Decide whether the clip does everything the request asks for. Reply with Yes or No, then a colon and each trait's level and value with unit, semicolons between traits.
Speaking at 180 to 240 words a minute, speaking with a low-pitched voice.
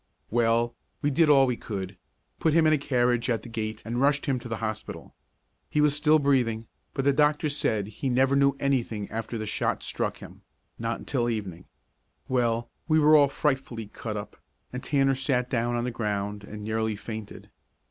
Yes: average, 190 wpm; low, 120 Hz